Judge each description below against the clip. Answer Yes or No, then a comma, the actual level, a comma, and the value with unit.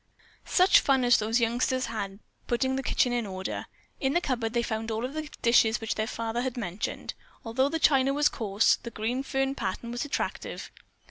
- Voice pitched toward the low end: No, high, 240 Hz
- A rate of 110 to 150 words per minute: No, average, 195 wpm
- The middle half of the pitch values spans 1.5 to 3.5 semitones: Yes, average, 3.1 semitones